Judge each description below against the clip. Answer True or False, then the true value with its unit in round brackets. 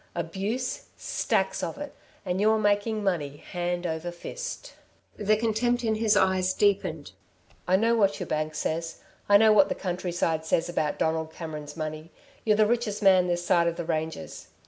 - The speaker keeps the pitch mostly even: False (4.6 semitones)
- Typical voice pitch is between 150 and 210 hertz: True (185 Hz)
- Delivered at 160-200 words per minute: True (170 wpm)